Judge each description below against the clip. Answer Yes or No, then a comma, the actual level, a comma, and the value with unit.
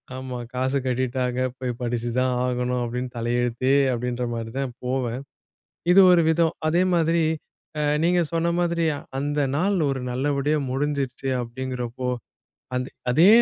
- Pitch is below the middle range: Yes, low, 130 Hz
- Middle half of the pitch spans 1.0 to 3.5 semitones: Yes, average, 3.0 semitones